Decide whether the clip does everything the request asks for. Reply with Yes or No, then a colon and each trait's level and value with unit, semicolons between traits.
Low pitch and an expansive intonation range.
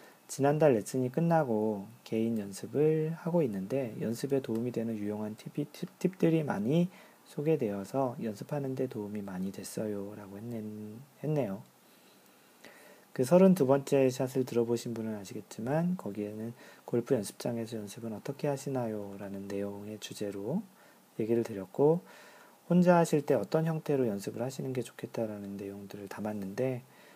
Yes: low, 120 Hz; wide, 5.8 semitones